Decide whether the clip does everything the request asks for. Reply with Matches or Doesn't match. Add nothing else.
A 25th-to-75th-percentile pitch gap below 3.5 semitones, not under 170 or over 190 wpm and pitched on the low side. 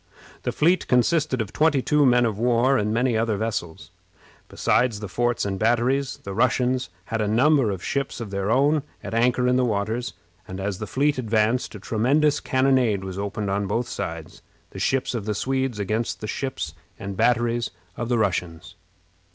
Doesn't match